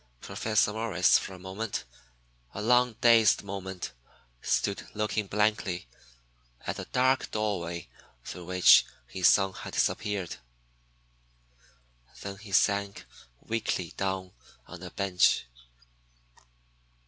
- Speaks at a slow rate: Yes, slow, 105 wpm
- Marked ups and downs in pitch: No, average, 2.7 semitones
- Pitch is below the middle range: Yes, low, 100 Hz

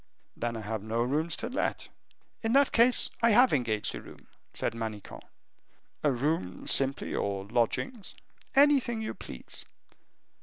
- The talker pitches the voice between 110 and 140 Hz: Yes, low, 135 Hz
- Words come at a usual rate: Yes, average, 145 wpm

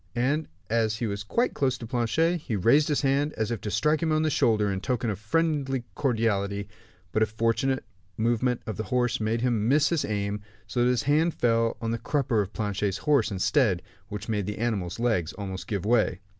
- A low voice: Yes, low, 115 Hz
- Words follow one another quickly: Yes, fast, 210 wpm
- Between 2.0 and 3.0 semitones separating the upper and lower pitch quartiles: No, average, 4.4 semitones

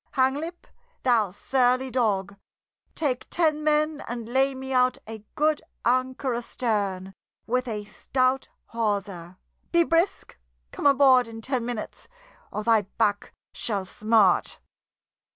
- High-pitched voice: Yes, very high, 250 Hz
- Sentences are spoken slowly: Yes, slow, 120 wpm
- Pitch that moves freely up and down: No, average, 3.9 semitones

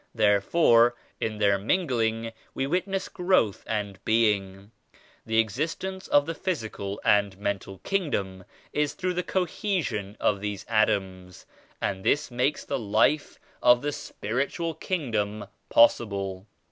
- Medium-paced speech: No, slow, 125 wpm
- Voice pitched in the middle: No, low, 115 Hz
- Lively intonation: Yes, wide, 6.9 semitones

